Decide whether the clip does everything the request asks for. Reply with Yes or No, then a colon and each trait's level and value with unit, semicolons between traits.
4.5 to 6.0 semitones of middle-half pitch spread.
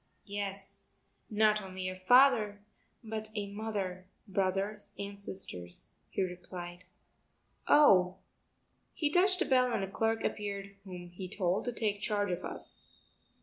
No: average, 2.7 semitones